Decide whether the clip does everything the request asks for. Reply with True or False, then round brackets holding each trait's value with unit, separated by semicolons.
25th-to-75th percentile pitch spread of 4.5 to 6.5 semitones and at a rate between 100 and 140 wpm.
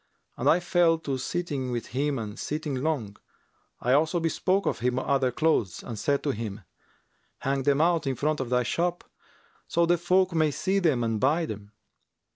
False (5.0 semitones; 185 wpm)